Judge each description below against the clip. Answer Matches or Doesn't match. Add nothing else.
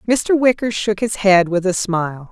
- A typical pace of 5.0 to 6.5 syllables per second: Doesn't match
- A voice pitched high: Matches